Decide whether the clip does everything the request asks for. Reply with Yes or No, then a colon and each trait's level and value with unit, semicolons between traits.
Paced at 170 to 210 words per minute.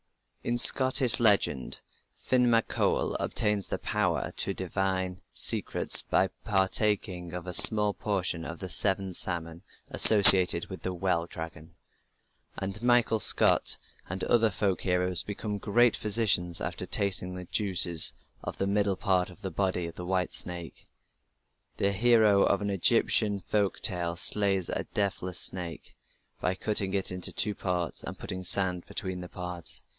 No: average, 150 wpm